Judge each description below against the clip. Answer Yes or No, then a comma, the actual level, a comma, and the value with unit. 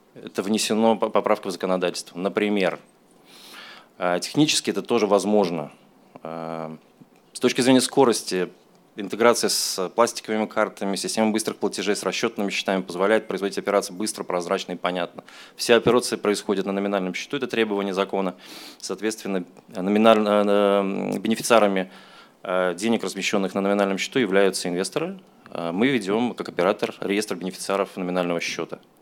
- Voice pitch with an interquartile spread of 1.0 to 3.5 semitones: Yes, average, 2.9 semitones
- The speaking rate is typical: Yes, average, 120 wpm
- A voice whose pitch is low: Yes, low, 100 Hz